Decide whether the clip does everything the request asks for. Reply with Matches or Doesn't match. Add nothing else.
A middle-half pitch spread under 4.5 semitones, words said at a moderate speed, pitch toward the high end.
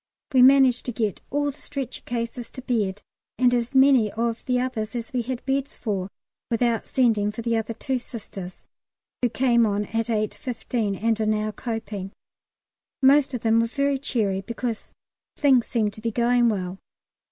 Matches